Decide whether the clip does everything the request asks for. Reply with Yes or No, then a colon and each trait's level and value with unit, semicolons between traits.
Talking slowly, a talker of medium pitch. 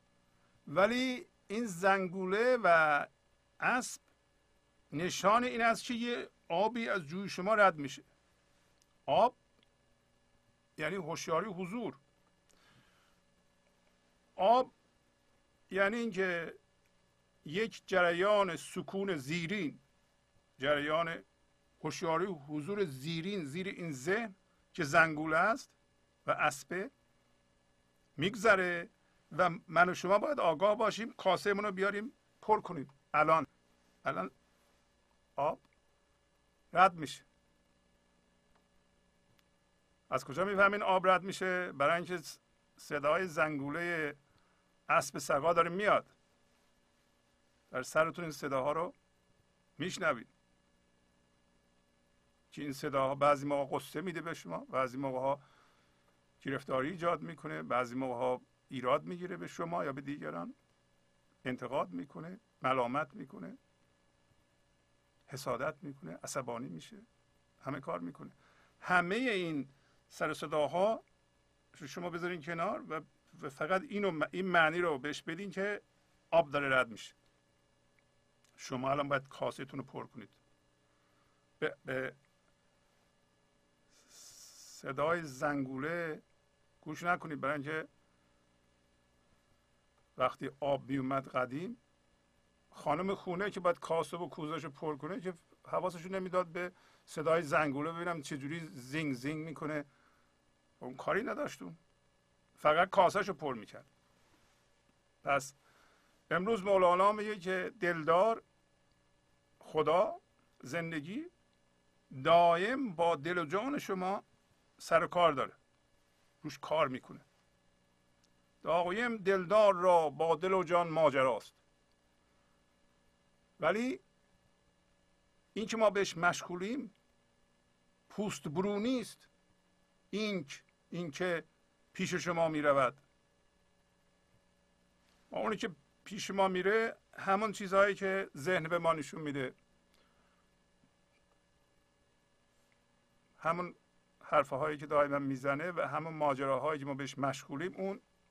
Yes: slow, 100 wpm; medium, 155 Hz